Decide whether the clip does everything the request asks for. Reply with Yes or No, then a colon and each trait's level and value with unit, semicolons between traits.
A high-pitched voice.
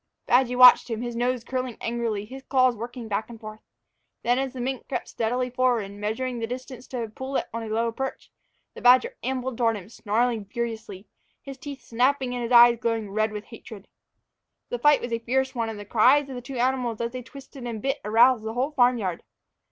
Yes: high, 240 Hz